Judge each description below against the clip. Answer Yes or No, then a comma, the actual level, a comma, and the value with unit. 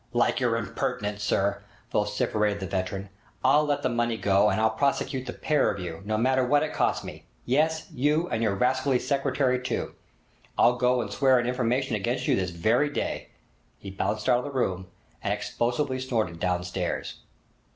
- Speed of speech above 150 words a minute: Yes, average, 180 wpm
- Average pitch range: Yes, average, 4.5 semitones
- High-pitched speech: No, low, 120 Hz